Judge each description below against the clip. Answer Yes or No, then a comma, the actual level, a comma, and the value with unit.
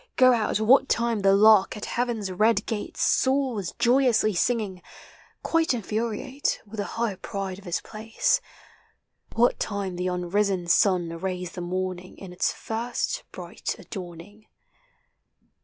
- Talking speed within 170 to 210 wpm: No, average, 140 wpm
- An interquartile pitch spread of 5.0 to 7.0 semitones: No, average, 4.1 semitones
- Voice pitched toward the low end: No, high, 210 Hz